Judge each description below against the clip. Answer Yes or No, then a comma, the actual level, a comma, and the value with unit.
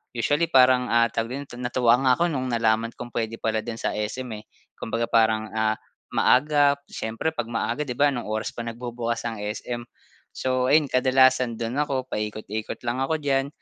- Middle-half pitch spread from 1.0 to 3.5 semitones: Yes, narrow, 2.6 semitones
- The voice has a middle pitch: No, low, 120 Hz